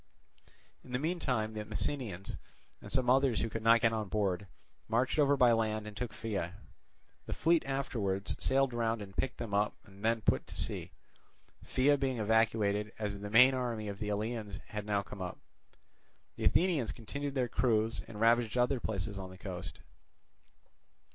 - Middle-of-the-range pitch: No, low, 110 Hz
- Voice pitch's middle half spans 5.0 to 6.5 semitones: No, average, 3.4 semitones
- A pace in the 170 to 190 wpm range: Yes, average, 175 wpm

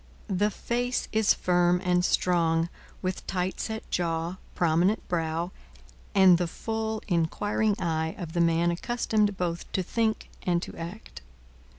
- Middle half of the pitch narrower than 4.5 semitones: Yes, average, 3.7 semitones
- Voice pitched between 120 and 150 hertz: No, medium, 180 Hz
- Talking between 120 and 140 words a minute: Yes, slow, 135 wpm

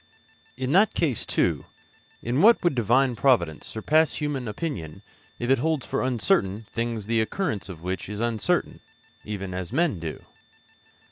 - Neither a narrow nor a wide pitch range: No, wide, 6.0 semitones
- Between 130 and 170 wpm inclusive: Yes, average, 150 wpm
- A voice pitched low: Yes, low, 120 Hz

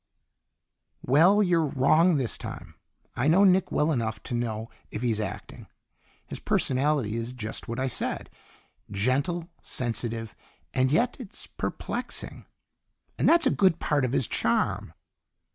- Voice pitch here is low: Yes, low, 130 Hz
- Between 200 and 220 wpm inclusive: No, average, 140 wpm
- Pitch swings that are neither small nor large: No, wide, 6.1 semitones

